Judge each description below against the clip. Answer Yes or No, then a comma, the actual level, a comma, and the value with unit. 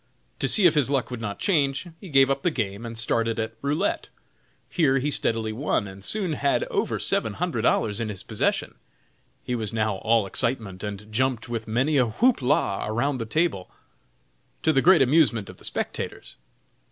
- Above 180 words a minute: Yes, average, 190 wpm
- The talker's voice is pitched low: Yes, low, 120 Hz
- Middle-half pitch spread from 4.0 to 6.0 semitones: Yes, average, 4.6 semitones